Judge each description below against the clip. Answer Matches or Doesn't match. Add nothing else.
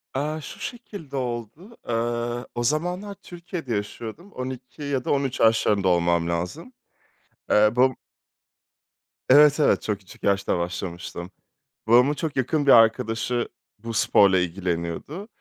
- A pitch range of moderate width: Doesn't match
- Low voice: Matches